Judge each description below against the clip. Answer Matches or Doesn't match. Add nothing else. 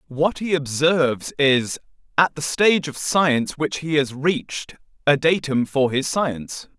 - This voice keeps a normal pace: Matches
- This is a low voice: Doesn't match